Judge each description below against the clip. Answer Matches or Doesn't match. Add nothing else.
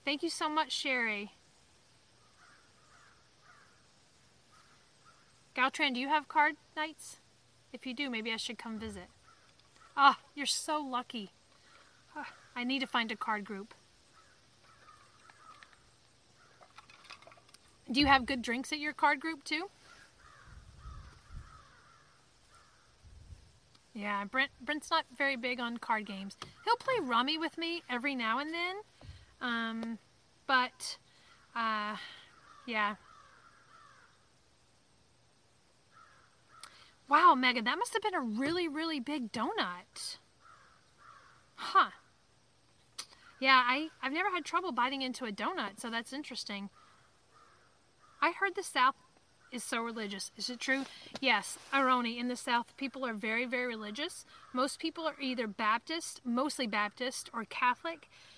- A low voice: Doesn't match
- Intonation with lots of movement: Doesn't match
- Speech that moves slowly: Matches